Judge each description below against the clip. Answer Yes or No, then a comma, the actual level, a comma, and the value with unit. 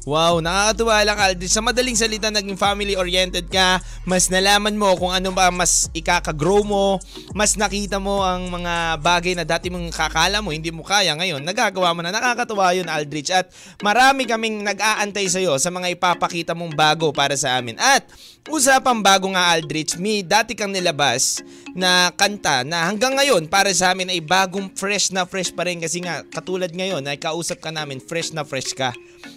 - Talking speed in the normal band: No, fast, 185 wpm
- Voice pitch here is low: No, medium, 185 Hz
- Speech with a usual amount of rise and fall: Yes, average, 3.2 semitones